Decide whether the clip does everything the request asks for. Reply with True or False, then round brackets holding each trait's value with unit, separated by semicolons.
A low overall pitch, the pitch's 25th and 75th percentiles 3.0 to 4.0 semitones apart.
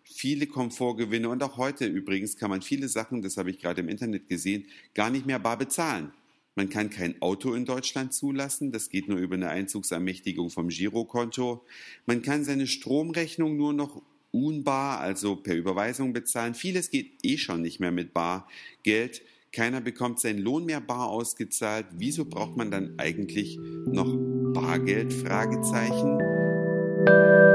False (120 Hz; 5.6 semitones)